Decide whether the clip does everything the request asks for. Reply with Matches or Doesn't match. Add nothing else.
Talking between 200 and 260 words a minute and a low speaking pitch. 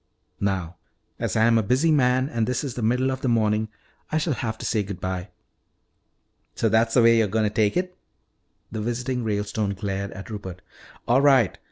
Matches